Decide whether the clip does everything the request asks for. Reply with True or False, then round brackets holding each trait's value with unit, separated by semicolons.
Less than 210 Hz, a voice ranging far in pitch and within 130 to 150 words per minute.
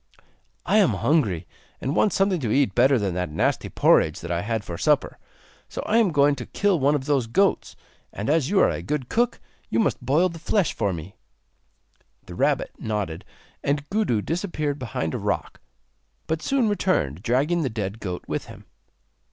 False (140 Hz; 8.9 semitones; 185 wpm)